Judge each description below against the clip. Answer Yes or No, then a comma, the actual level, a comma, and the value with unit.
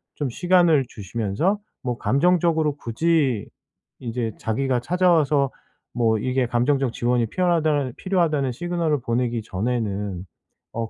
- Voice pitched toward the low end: Yes, low, 130 Hz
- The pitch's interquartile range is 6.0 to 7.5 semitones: No, wide, 5.6 semitones